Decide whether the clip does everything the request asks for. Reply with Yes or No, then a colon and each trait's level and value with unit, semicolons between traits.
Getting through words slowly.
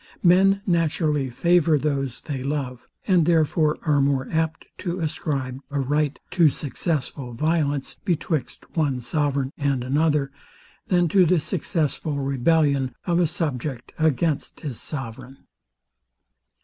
Yes: slow, 125 wpm